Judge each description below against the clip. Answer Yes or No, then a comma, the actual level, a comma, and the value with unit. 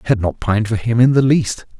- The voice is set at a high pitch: No, low, 115 Hz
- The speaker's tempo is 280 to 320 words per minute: Yes, fast, 300 wpm